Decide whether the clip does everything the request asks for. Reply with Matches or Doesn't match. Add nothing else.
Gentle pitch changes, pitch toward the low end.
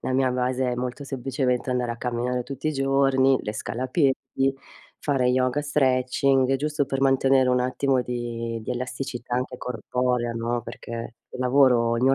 Matches